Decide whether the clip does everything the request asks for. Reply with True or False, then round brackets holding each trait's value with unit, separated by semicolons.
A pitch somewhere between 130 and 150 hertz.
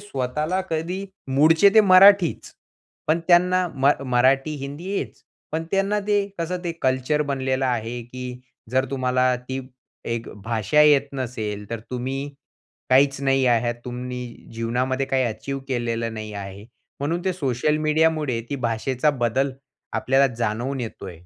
True (135 Hz)